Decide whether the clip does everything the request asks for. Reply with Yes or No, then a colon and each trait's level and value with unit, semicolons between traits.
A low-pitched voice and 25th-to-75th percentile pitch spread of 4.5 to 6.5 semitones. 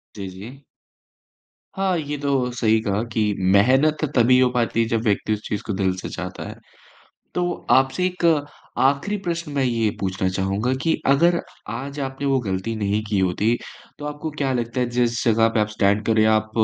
Yes: low, 120 Hz; average, 4.8 semitones